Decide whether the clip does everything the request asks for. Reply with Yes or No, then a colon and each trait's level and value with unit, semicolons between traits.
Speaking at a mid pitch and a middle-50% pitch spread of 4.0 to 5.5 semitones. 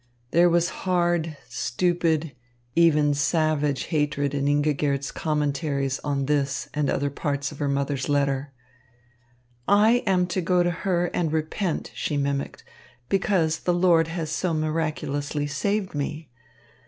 No: medium, 155 Hz; average, 3.3 semitones